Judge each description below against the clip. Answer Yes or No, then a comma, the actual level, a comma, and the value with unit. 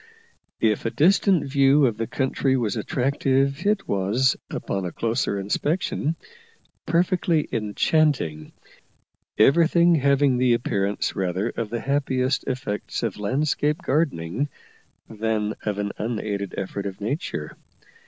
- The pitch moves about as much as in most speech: No, wide, 5.7 semitones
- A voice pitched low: Yes, low, 130 Hz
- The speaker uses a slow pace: Yes, slow, 120 wpm